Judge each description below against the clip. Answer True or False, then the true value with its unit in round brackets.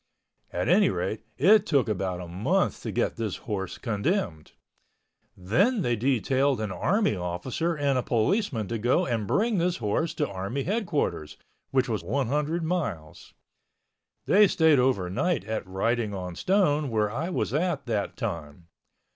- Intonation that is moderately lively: False (8.8 semitones)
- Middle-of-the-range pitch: False (125 Hz)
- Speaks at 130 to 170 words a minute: True (155 wpm)